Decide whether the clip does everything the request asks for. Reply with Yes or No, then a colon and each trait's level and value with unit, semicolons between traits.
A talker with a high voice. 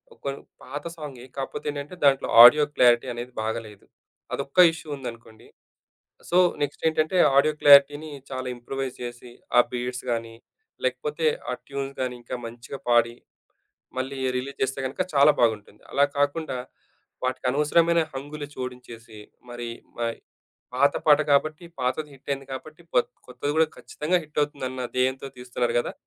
No: low, 135 Hz